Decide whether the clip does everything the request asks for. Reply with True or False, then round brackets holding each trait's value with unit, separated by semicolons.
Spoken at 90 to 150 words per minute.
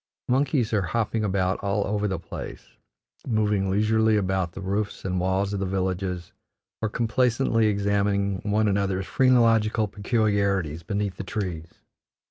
True (135 wpm)